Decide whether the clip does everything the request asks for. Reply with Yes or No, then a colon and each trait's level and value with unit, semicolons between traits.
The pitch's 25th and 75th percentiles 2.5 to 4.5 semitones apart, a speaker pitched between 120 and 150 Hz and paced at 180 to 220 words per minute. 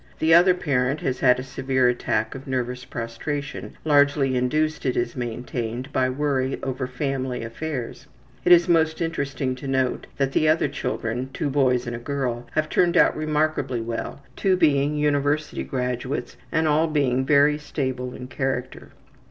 No: average, 3.0 semitones; low, 135 Hz; average, 160 wpm